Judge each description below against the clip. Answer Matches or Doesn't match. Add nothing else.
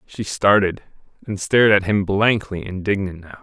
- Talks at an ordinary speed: Matches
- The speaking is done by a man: Matches